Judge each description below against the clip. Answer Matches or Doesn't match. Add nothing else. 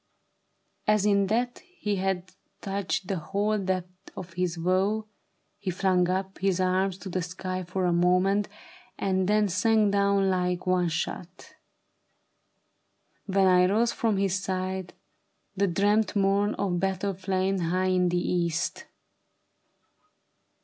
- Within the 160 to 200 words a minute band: Doesn't match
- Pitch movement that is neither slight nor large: Doesn't match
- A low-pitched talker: Doesn't match